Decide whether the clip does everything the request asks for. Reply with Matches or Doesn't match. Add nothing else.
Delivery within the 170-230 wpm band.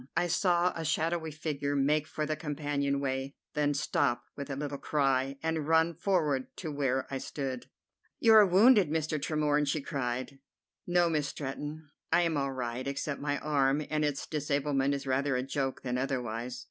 Matches